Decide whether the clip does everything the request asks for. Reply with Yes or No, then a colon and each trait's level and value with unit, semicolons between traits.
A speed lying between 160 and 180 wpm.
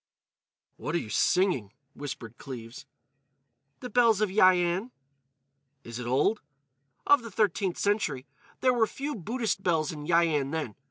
No: average, 145 wpm